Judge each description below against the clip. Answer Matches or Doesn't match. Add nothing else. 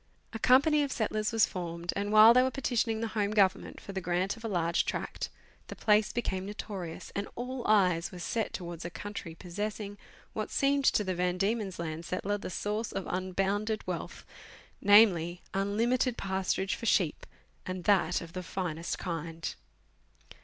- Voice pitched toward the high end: Matches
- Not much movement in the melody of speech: Doesn't match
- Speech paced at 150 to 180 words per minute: Matches